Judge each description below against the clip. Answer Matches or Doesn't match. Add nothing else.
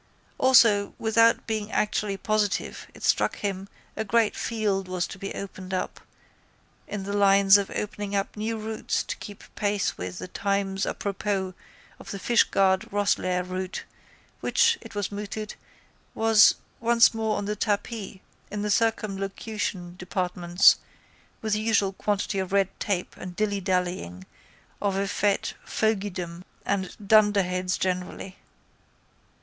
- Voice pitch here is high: Matches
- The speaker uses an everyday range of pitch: Doesn't match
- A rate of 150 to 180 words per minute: Doesn't match